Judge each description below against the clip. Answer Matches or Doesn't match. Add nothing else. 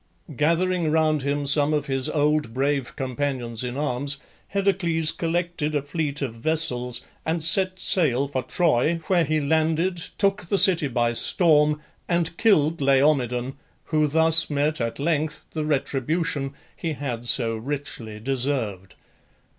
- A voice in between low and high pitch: Matches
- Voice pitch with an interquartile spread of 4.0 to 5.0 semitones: Doesn't match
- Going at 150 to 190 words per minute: Doesn't match